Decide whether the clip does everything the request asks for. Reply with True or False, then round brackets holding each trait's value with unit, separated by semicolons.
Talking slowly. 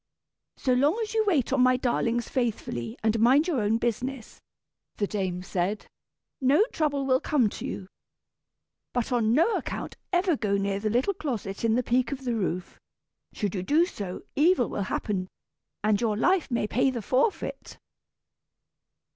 False (165 wpm)